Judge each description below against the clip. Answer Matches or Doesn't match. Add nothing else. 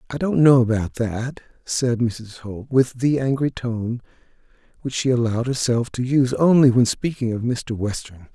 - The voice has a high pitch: Doesn't match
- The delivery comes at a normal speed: Matches